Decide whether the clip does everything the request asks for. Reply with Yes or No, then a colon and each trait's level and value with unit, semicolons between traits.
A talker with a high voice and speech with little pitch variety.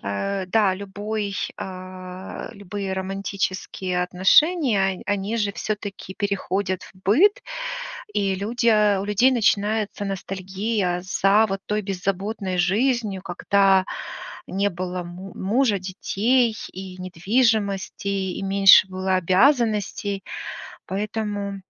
Yes: high, 195 Hz; narrow, 2.1 semitones